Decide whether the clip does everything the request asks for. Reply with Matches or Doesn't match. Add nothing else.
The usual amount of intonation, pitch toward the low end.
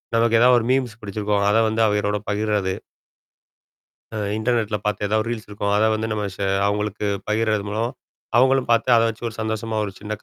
Doesn't match